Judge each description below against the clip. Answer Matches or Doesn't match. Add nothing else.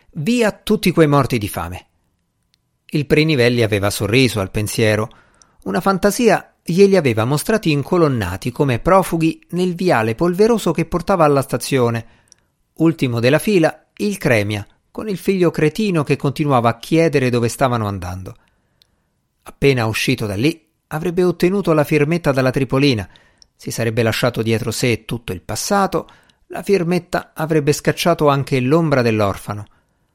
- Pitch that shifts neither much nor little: Doesn't match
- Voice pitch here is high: Doesn't match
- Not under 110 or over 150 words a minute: Matches